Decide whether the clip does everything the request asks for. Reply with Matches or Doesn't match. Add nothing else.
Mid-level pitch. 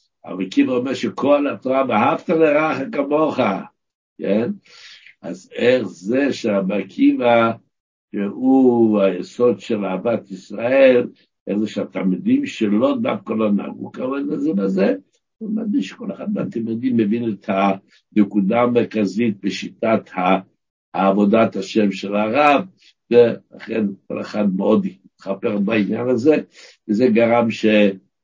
Doesn't match